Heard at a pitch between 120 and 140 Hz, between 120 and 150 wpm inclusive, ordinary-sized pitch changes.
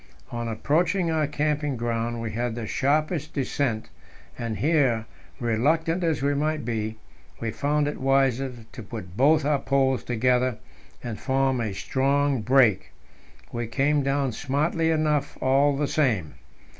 Yes: low, 135 Hz; average, 145 wpm; average, 3.9 semitones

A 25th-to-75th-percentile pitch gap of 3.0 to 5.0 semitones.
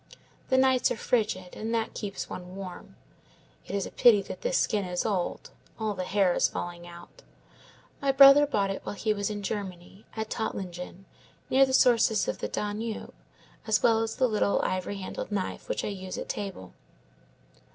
Yes: average, 3.4 semitones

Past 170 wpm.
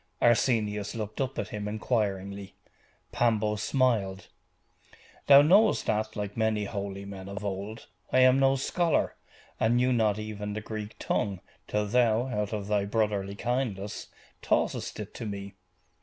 No: average, 145 wpm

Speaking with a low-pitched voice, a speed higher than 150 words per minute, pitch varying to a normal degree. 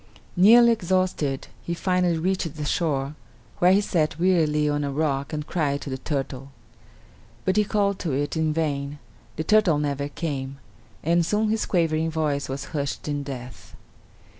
No: medium, 155 Hz; average, 165 wpm; average, 4.2 semitones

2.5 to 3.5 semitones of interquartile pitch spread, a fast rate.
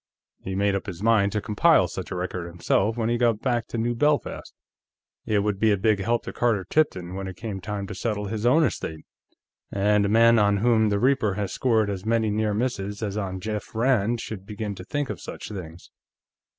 Yes: average, 2.9 semitones; fast, 215 wpm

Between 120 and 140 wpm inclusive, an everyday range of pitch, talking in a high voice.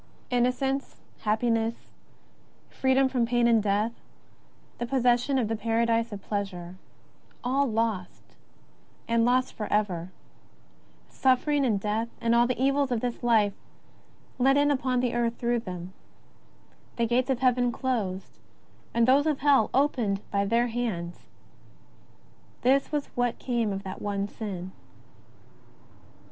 Yes: slow, 135 wpm; average, 3.4 semitones; high, 235 Hz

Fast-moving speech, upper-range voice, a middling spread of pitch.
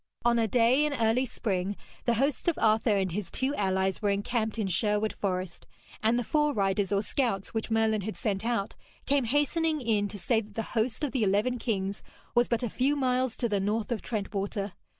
Yes: fast, 210 wpm; high, 220 Hz; average, 3.7 semitones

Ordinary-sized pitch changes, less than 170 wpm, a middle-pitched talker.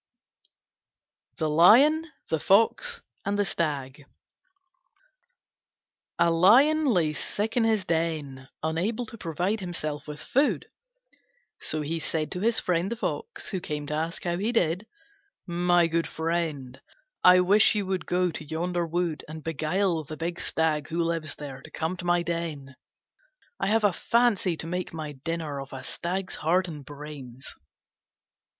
Yes: average, 3.7 semitones; average, 155 wpm; medium, 170 Hz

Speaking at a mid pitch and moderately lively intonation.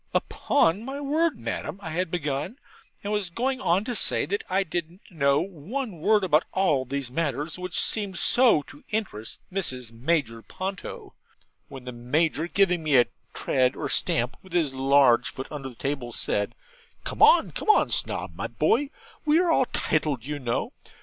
No: medium, 165 Hz; wide, 6.7 semitones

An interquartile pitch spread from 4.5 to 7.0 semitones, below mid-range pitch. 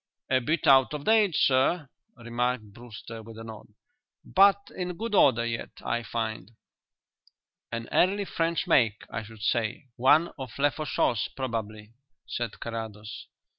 Yes: average, 5.2 semitones; low, 120 Hz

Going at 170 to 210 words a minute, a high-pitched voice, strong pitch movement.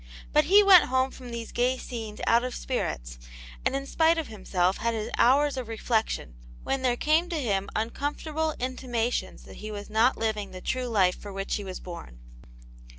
No: average, 190 wpm; high, 240 Hz; average, 4.4 semitones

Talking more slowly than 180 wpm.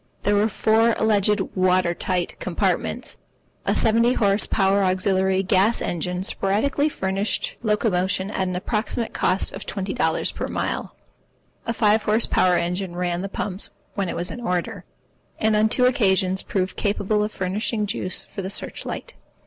Yes: average, 160 wpm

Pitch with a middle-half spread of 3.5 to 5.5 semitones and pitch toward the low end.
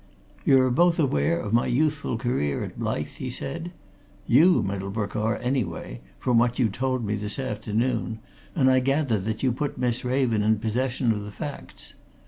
Yes: average, 3.9 semitones; low, 120 Hz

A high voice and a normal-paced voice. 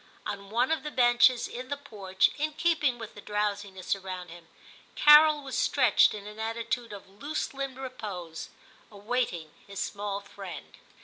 Yes: high, 220 Hz; average, 165 wpm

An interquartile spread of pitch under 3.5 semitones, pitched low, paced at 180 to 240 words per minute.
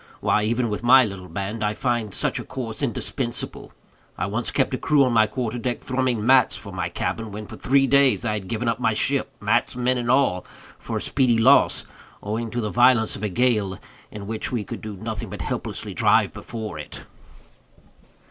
Yes: average, 3.0 semitones; low, 115 Hz; average, 195 wpm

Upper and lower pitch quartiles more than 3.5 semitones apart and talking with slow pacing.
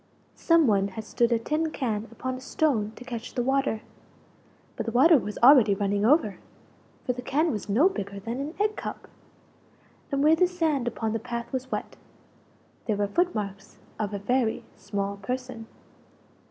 No: average, 4.9 semitones; average, 180 wpm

